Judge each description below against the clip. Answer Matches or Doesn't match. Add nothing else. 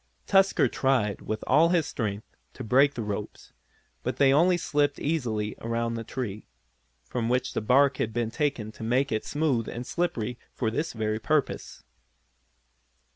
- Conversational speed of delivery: Matches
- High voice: Doesn't match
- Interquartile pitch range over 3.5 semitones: Matches